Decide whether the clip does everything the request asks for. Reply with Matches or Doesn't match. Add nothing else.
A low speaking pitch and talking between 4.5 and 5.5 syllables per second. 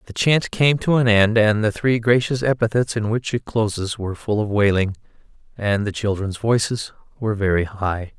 Matches